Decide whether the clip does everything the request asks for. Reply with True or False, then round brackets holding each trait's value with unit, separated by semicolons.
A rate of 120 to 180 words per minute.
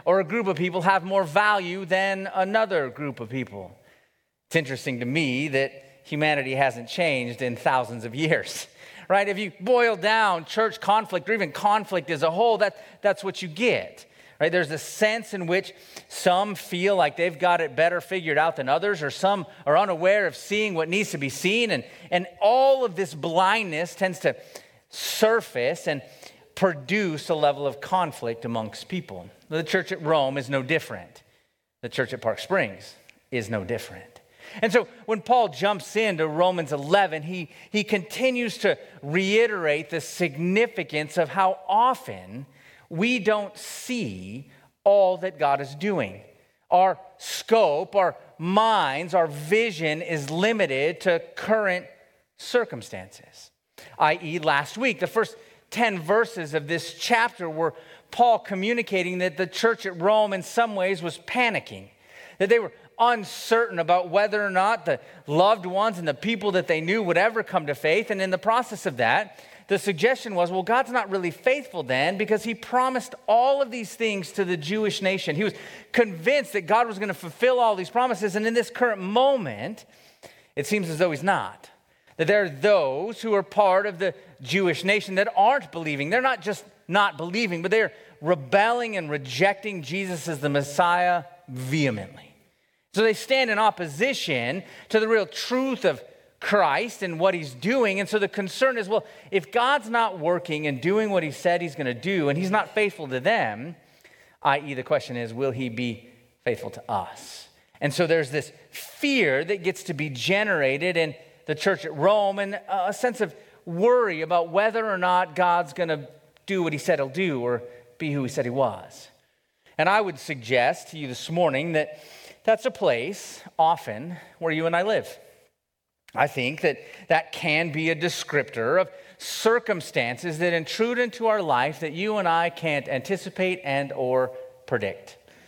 True (175 wpm)